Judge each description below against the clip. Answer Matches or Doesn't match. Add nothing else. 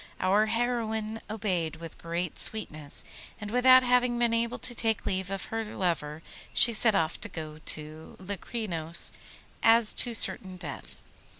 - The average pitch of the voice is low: Doesn't match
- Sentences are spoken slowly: Doesn't match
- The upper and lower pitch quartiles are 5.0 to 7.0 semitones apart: Matches